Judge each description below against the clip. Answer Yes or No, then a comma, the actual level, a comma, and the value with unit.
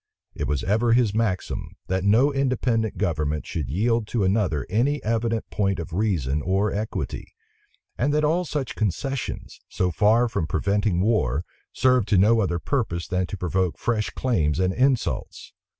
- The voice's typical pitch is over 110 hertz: No, low, 105 Hz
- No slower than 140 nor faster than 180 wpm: Yes, average, 160 wpm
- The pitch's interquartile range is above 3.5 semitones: Yes, average, 4.6 semitones